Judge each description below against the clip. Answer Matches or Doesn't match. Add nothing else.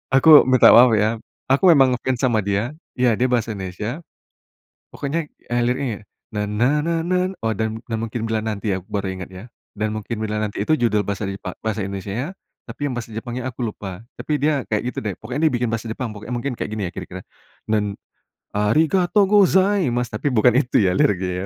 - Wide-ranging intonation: Doesn't match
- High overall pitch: Doesn't match